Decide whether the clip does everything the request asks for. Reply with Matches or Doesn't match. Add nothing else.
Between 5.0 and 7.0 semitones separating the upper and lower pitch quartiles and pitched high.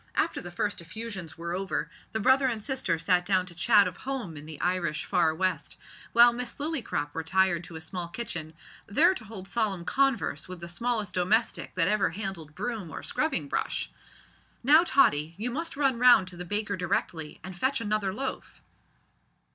Matches